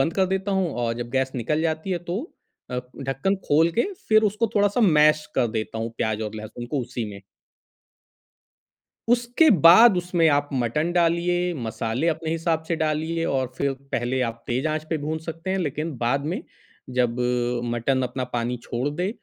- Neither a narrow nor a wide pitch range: No, wide, 5.8 semitones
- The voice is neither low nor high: Yes, medium, 155 Hz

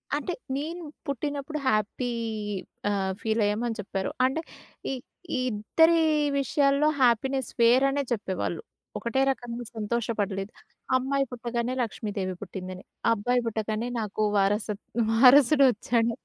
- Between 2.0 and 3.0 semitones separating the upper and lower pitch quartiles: No, average, 4.2 semitones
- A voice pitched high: Yes, high, 235 Hz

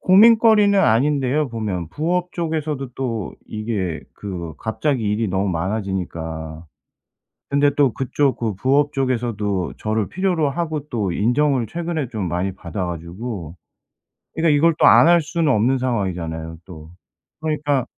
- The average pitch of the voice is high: No, low, 120 Hz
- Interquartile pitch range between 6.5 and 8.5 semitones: Yes, wide, 7.8 semitones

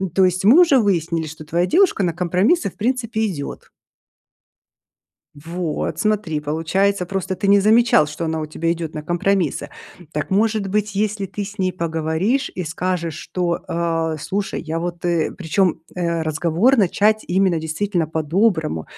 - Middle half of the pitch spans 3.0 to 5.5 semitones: Yes, average, 3.9 semitones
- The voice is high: No, medium, 175 Hz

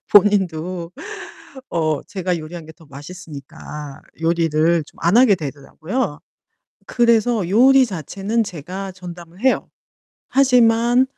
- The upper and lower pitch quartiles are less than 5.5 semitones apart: No, wide, 5.8 semitones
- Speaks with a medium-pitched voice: Yes, medium, 180 Hz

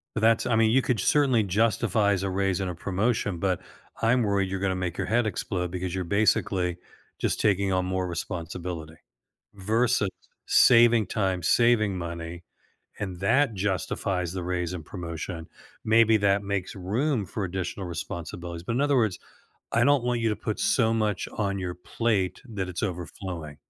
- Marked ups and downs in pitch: No, average, 3.7 semitones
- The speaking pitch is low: Yes, very low, 95 Hz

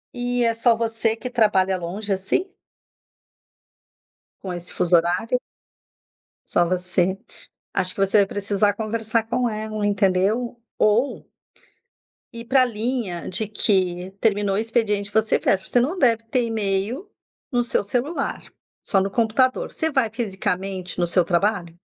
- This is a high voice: Yes, high, 215 Hz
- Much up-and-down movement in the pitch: No, average, 3.5 semitones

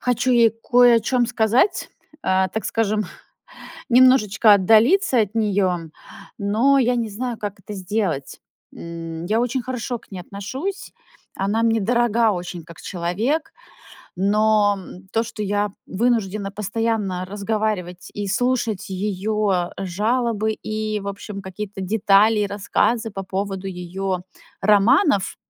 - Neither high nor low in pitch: No, high, 210 Hz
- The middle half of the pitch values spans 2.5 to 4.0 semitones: Yes, average, 3.1 semitones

